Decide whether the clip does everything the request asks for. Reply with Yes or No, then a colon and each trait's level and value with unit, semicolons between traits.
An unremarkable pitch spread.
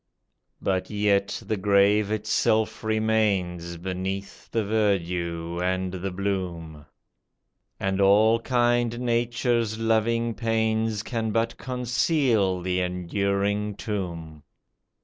Yes: average, 3.4 semitones